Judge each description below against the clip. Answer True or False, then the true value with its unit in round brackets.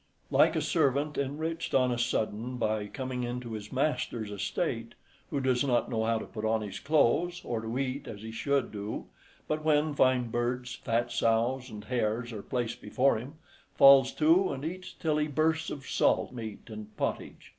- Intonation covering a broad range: False (3.9 semitones)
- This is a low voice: True (125 Hz)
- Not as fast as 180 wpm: False (185 wpm)